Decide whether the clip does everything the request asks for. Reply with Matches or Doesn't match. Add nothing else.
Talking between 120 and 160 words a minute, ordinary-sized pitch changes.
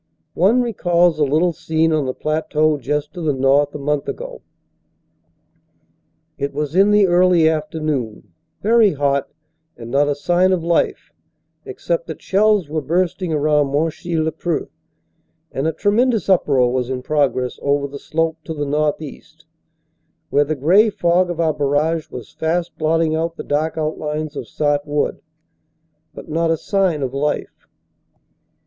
Matches